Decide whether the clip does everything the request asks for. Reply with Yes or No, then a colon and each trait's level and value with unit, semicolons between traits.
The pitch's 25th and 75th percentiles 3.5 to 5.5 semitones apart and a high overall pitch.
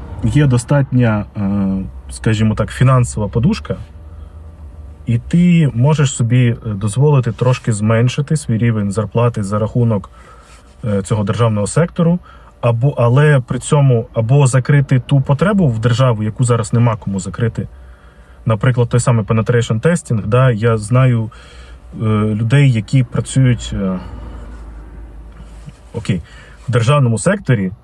No: average, 4.1 semitones; low, 115 Hz